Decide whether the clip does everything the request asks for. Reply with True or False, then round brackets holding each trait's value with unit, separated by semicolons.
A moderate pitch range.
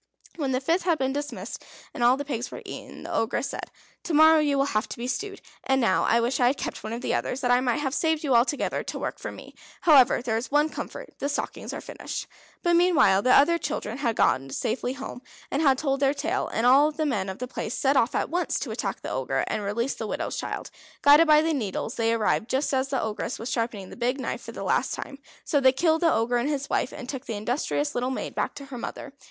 True (3.6 semitones)